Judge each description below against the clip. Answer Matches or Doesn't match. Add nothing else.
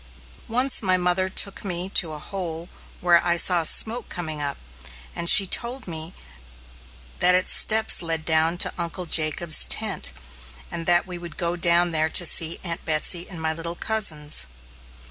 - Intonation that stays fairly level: Matches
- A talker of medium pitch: Matches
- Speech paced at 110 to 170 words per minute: Matches